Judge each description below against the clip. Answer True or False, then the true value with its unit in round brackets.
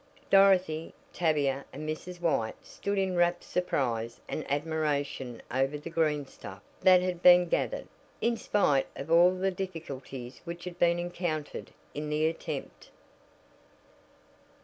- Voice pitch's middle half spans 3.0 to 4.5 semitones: True (3.9 semitones)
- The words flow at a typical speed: False (125 wpm)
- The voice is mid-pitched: True (165 Hz)